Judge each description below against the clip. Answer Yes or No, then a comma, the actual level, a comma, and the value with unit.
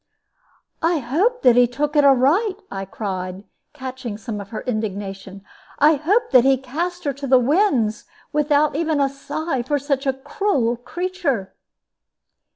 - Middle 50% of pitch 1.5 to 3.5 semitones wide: No, average, 4.8 semitones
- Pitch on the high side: Yes, very high, 270 Hz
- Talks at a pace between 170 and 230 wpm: No, average, 155 wpm